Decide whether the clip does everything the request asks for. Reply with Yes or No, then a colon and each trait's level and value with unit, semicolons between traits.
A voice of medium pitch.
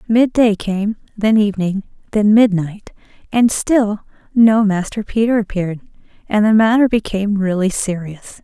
No: high, 210 Hz